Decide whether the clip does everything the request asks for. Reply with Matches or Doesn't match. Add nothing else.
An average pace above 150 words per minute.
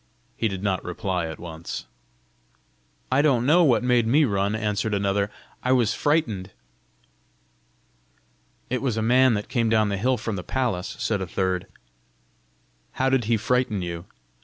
Matches